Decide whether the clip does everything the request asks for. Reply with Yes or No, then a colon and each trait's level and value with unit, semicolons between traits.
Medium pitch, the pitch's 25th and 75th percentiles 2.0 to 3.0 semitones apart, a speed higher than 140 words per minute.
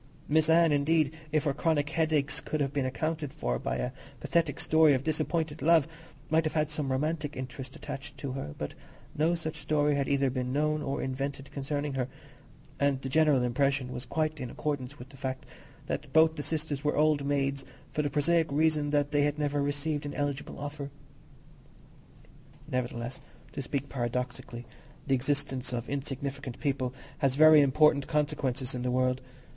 Yes: medium, 145 Hz; narrow, 2.4 semitones; average, 175 wpm